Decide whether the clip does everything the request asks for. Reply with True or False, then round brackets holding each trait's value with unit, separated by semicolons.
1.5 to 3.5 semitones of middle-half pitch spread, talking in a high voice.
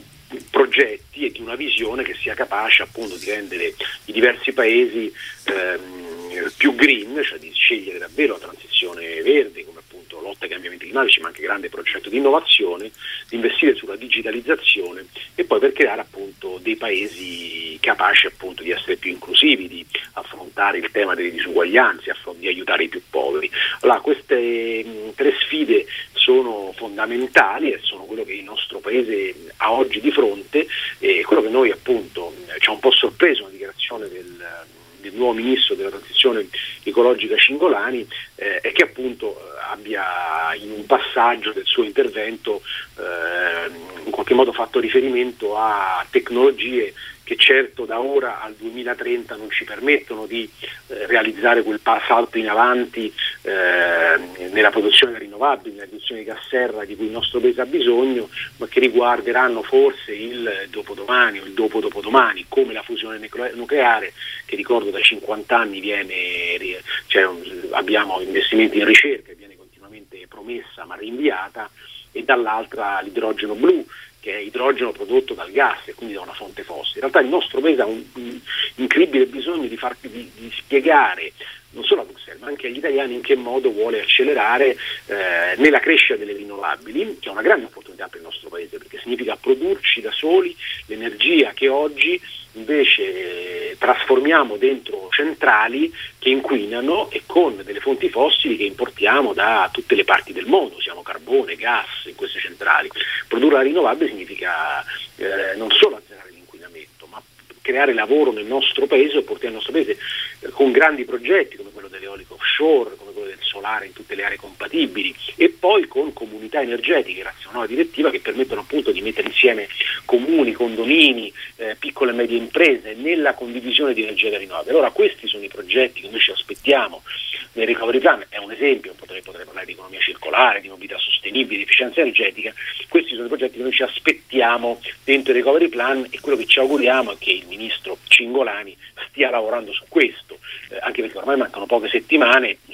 True (2.6 semitones; 395 Hz)